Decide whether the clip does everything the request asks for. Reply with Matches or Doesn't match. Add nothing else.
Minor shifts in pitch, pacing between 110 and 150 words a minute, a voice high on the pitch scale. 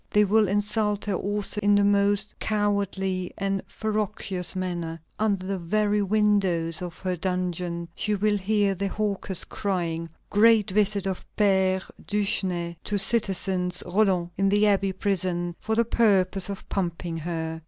Matches